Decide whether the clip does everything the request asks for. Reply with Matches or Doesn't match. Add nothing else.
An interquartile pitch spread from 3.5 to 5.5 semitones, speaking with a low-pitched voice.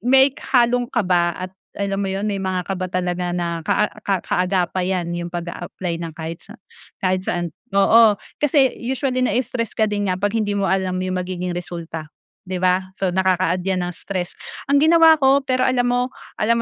Doesn't match